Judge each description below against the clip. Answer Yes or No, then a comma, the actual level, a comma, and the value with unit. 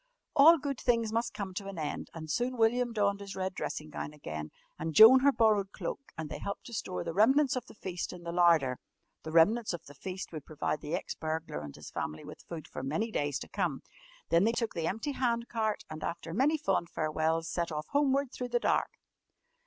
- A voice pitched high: Yes, high, 195 Hz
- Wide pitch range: Yes, wide, 6.6 semitones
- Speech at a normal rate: No, fast, 225 wpm